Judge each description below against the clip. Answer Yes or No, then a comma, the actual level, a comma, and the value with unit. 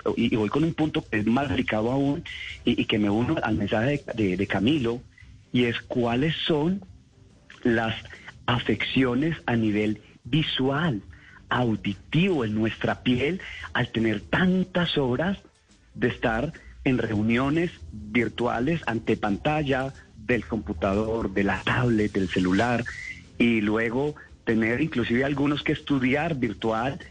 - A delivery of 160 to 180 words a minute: No, average, 135 wpm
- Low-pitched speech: Yes, low, 120 Hz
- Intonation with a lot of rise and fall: No, average, 4.4 semitones